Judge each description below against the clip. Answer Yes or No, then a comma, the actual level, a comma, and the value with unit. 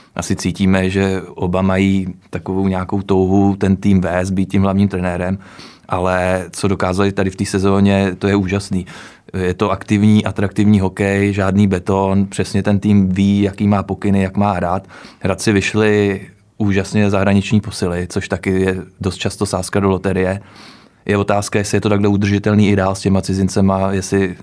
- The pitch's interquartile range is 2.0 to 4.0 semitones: No, narrow, 1.1 semitones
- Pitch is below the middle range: Yes, low, 100 Hz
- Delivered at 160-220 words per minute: Yes, average, 165 wpm